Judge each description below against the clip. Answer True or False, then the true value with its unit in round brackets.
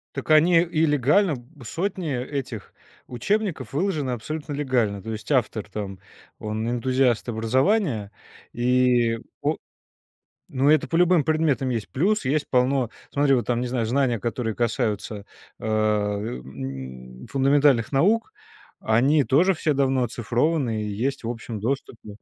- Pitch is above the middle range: False (125 Hz)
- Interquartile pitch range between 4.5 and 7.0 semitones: True (4.9 semitones)